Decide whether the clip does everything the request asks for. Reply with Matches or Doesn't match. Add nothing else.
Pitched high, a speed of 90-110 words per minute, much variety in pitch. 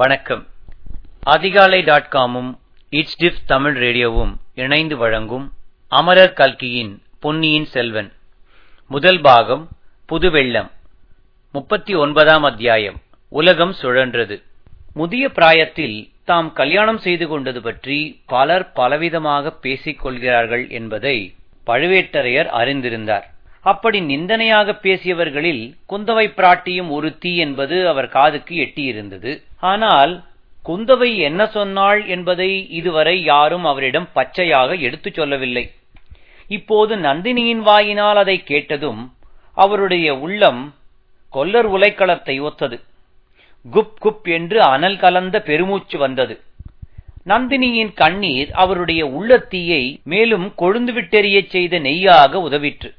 Doesn't match